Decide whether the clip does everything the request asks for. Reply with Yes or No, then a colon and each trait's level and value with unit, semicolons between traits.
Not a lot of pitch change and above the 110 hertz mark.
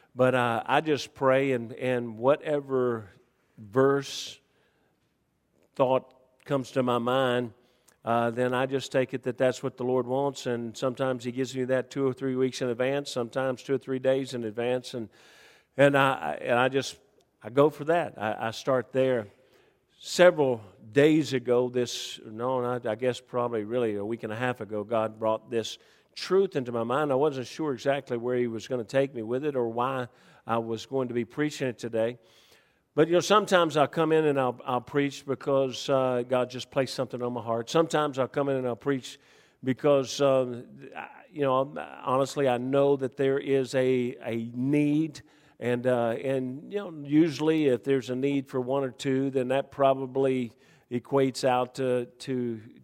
Yes: narrow, 2.1 semitones; low, 130 Hz